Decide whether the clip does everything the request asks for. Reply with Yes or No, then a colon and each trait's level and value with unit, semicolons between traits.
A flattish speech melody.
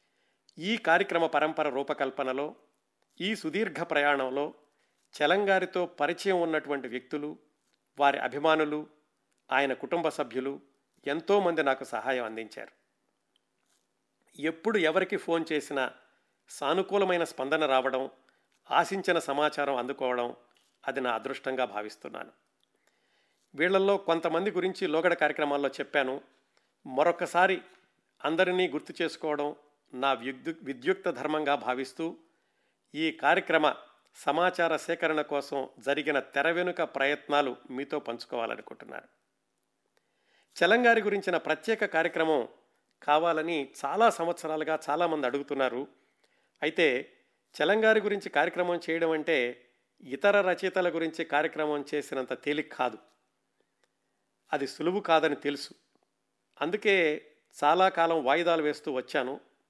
No: average, 3.8 semitones